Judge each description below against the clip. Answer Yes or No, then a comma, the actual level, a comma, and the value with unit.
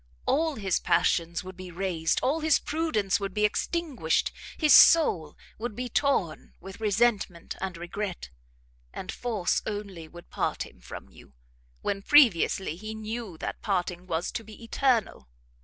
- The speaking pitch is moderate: No, high, 200 Hz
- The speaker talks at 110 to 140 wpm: No, average, 150 wpm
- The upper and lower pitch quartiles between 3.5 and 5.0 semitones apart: No, wide, 5.4 semitones